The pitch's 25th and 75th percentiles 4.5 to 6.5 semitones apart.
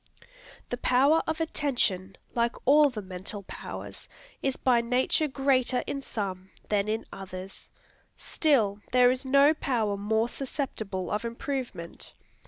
Yes: average, 5.2 semitones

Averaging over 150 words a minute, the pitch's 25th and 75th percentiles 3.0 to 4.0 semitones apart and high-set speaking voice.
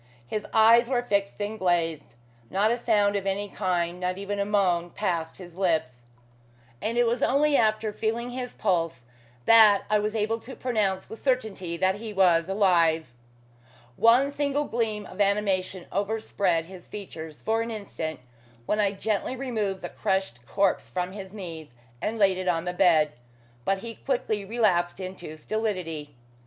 Yes: average, 165 wpm; average, 3.7 semitones; high, 200 Hz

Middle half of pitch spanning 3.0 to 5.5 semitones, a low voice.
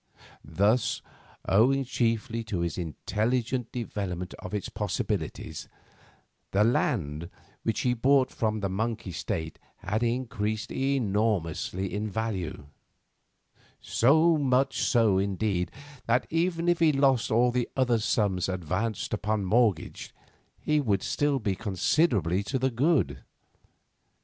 Yes: average, 4.8 semitones; low, 110 Hz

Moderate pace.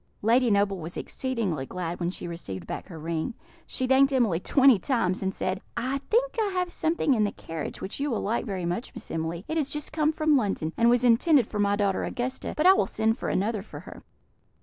No: fast, 225 wpm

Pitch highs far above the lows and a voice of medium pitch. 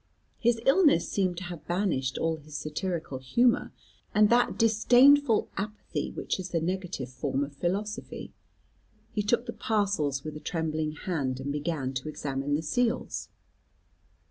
Yes: wide, 6.5 semitones; medium, 175 Hz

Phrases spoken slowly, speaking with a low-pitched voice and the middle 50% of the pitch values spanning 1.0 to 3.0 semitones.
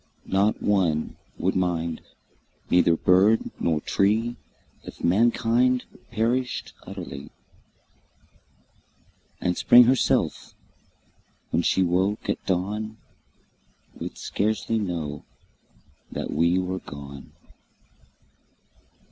No: slow, 85 wpm; very low, 95 Hz; average, 4.5 semitones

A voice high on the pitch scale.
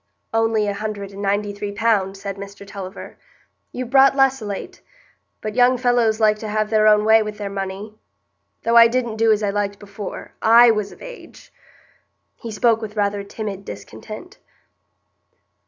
Yes: high, 215 Hz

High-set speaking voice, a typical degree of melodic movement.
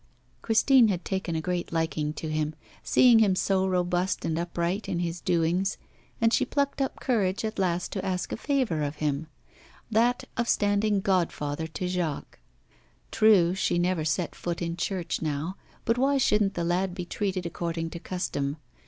No: medium, 180 Hz; average, 3.6 semitones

